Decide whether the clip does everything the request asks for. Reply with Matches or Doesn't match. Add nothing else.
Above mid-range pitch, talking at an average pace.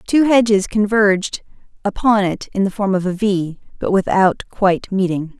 Matches